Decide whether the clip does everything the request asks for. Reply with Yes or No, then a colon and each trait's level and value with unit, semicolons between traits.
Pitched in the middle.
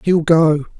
Yes: medium, 160 Hz